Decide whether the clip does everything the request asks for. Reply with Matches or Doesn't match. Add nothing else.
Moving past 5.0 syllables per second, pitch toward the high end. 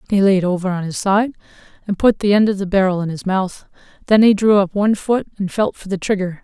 Matches